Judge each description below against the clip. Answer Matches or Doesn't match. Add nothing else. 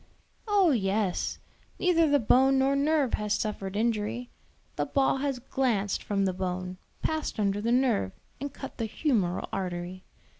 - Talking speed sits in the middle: Matches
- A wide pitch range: Matches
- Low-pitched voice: Doesn't match